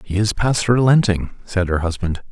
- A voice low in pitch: Yes, low, 100 Hz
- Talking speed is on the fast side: No, average, 180 wpm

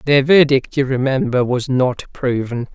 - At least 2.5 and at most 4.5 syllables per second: Yes, 4.4 syllables/s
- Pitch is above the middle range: No, low, 130 Hz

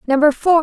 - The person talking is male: No, female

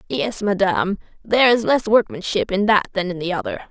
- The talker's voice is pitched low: No, high, 200 Hz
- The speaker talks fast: No, average, 195 wpm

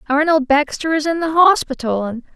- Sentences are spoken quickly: No, average, 180 wpm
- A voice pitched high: Yes, very high, 295 Hz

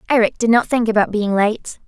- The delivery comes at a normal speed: No, fast, 225 wpm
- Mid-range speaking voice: No, high, 220 Hz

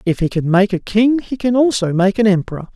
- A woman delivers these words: No, male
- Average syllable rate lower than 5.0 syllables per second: No, 5.8 syllables/s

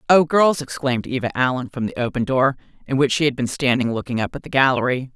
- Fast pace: Yes, fast, 235 wpm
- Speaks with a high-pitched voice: No, low, 130 Hz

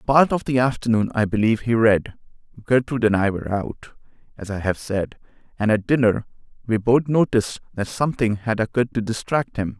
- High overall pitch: No, low, 115 Hz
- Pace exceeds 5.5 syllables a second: Yes, 5.7 syllables/s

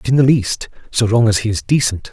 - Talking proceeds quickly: Yes, fast, 285 wpm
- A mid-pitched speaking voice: No, low, 115 Hz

